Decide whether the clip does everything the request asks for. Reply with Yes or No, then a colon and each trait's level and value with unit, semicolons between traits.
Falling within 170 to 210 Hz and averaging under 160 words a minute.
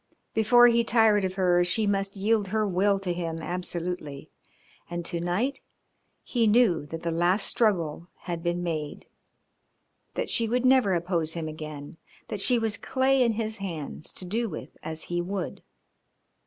No: medium, 185 Hz; average, 165 wpm